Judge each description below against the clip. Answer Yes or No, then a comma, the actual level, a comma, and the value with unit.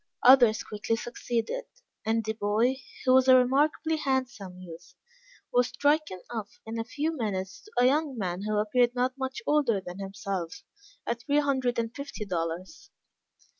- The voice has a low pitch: No, high, 235 Hz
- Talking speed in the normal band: Yes, average, 160 wpm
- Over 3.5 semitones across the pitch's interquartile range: Yes, average, 4.3 semitones